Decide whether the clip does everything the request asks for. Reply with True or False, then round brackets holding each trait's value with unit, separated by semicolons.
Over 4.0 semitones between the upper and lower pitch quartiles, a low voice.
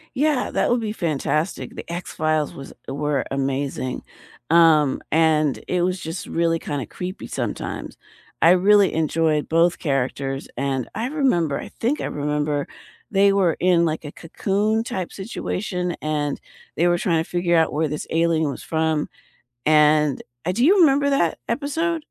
False (4.4 semitones; 165 Hz)